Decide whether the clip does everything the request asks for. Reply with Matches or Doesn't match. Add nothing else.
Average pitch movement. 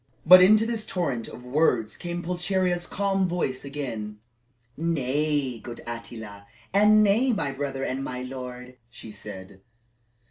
Doesn't match